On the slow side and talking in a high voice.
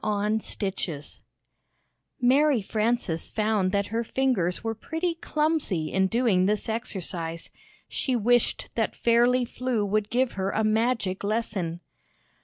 Yes: slow, 130 wpm; high, 220 Hz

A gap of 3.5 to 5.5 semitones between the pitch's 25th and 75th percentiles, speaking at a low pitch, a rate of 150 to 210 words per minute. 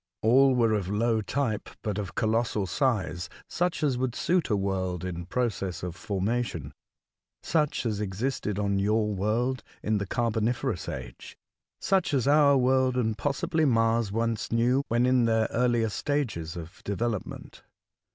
Yes: average, 4.1 semitones; low, 115 Hz; average, 160 wpm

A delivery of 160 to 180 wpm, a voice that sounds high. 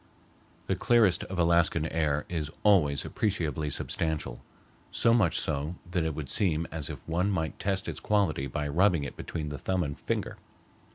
No: average, 170 wpm; very low, 80 Hz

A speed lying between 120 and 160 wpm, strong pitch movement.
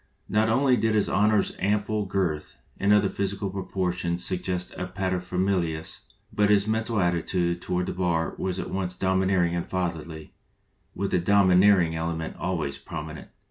No: average, 155 wpm; narrow, 2.6 semitones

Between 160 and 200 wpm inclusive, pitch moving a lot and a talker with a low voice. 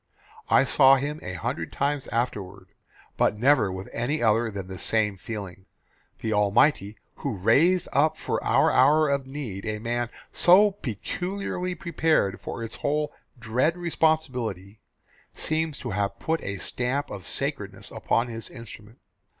No: average, 145 wpm; wide, 6.4 semitones; low, 120 Hz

